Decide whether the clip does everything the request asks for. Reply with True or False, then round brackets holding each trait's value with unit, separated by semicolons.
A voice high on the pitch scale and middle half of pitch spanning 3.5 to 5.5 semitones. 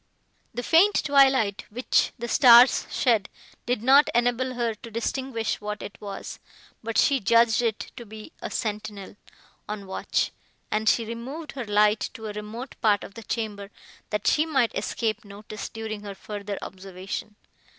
False (225 Hz; 2.7 semitones)